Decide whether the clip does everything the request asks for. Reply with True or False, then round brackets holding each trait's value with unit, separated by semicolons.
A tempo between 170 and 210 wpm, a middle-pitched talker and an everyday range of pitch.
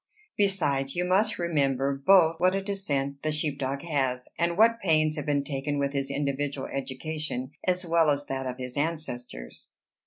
True (175 wpm; 145 Hz; 3.7 semitones)